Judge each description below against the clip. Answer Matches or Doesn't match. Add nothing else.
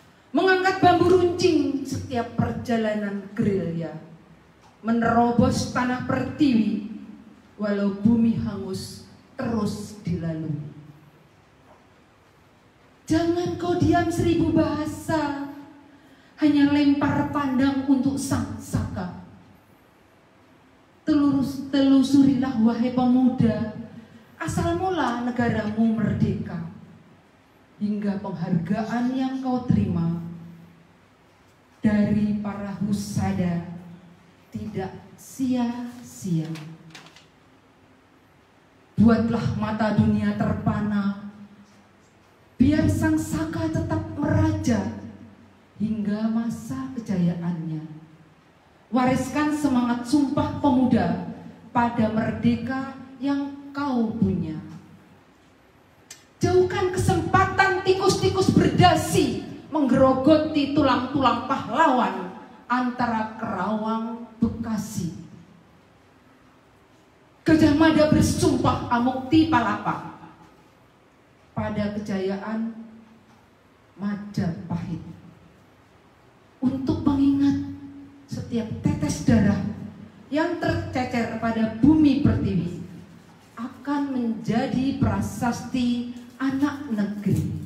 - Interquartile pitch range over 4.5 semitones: Matches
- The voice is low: Doesn't match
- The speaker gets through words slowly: Matches